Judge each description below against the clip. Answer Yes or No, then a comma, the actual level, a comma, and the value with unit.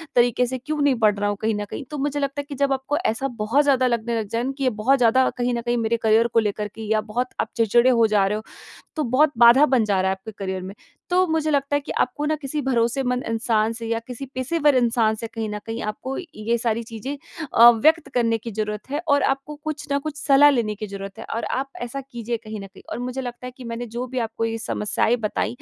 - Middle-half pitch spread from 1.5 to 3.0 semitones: No, average, 3.6 semitones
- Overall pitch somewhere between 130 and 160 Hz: No, high, 240 Hz